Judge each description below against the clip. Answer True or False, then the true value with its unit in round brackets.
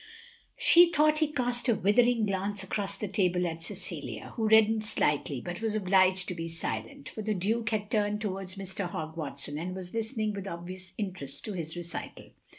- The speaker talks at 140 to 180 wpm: False (190 wpm)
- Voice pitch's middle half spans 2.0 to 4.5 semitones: True (3.8 semitones)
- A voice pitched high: True (195 Hz)